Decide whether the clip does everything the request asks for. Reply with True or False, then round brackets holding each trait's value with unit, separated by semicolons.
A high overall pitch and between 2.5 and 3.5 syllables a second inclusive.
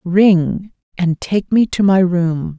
False (180 Hz; 3.1 syllables/s)